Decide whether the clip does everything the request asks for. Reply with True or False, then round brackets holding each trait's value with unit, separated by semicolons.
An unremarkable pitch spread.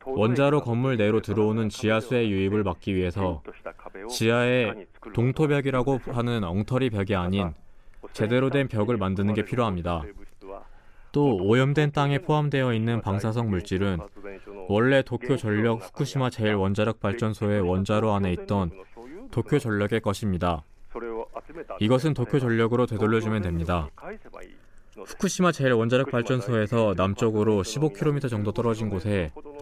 True (4.0 semitones)